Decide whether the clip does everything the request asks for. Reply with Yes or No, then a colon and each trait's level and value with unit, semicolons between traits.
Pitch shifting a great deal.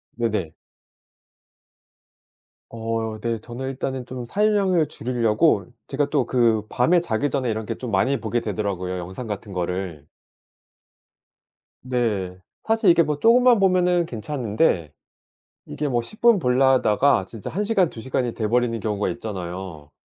Yes: wide, 5.7 semitones